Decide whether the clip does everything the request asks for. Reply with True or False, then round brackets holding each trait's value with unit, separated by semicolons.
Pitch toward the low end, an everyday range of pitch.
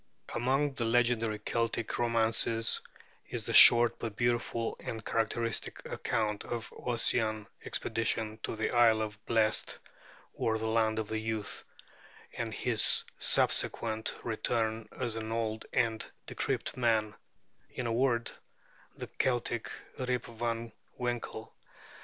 False (115 Hz; 1.3 semitones)